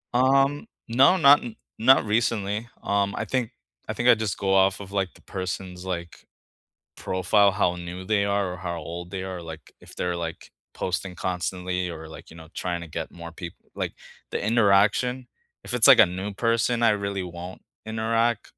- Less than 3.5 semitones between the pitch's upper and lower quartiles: No, average, 4.0 semitones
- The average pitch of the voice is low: Yes, low, 100 Hz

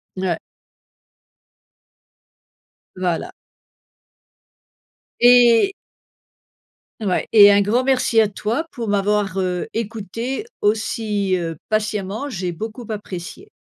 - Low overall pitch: No, high, 210 Hz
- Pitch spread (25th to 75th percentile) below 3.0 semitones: No, average, 3.3 semitones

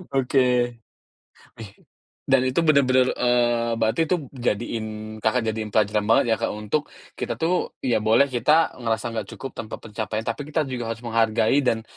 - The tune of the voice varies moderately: Yes, average, 3.2 semitones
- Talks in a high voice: No, low, 120 Hz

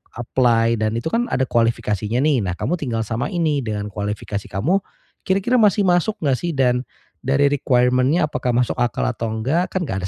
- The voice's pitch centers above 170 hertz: No, low, 125 Hz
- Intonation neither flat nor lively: No, wide, 6.0 semitones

